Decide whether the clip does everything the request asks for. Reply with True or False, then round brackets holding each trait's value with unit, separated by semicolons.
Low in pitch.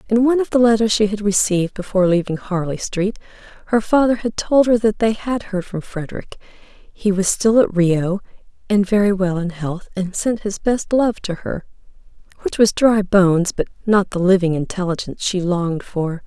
False (200 Hz)